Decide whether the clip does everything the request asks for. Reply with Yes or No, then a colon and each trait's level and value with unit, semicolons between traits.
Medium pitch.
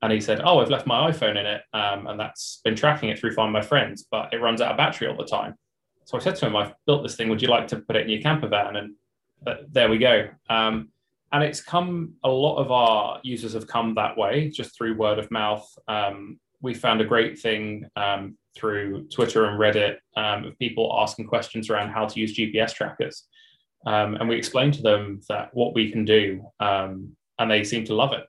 No: low, 110 Hz